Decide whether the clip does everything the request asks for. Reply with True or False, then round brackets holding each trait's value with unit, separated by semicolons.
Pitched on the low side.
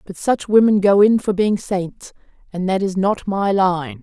False (190 Hz)